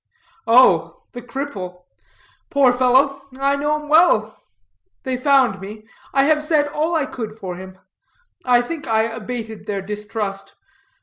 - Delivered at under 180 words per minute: Yes, average, 140 wpm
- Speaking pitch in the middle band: No, high, 245 Hz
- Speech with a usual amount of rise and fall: Yes, average, 5.0 semitones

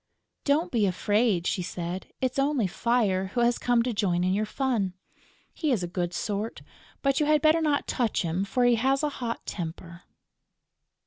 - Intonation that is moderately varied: No, wide, 6.0 semitones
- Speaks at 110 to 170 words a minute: No, average, 185 wpm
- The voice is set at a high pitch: Yes, high, 230 Hz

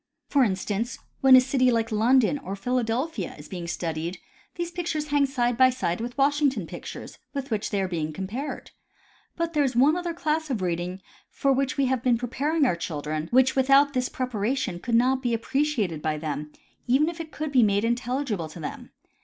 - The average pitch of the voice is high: Yes, very high, 250 Hz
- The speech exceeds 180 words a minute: Yes, average, 195 wpm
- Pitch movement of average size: No, wide, 6.0 semitones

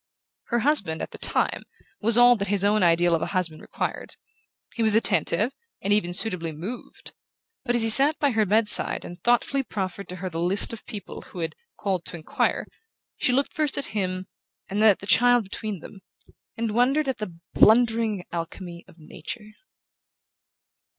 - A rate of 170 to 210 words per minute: Yes, average, 180 wpm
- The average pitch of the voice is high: Yes, high, 210 Hz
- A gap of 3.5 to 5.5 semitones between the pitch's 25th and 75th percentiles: Yes, average, 4.5 semitones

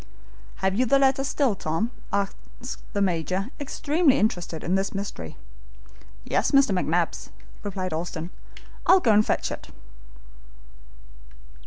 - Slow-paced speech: Yes, slow, 125 wpm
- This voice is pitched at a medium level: No, high, 200 Hz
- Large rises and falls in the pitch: Yes, wide, 6.4 semitones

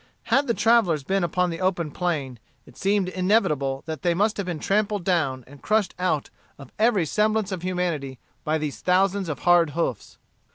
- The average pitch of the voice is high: No, medium, 180 Hz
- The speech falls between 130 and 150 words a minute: No, average, 180 wpm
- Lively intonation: No, average, 4.4 semitones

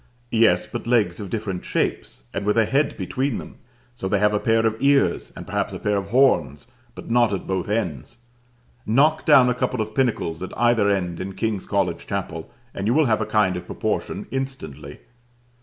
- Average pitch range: Yes, average, 4.2 semitones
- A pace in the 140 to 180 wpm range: No, average, 200 wpm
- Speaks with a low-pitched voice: Yes, low, 110 Hz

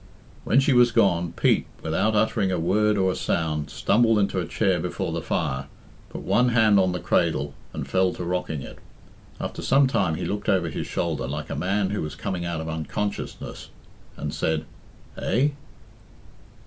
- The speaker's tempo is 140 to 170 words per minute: No, average, 180 wpm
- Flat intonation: No, average, 4.5 semitones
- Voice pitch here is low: Yes, very low, 95 Hz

